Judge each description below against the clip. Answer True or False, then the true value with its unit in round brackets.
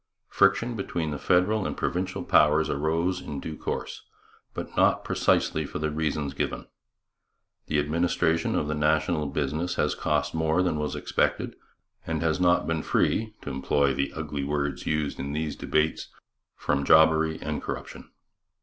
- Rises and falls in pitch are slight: True (2.0 semitones)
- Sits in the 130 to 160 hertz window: False (80 Hz)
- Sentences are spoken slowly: False (155 wpm)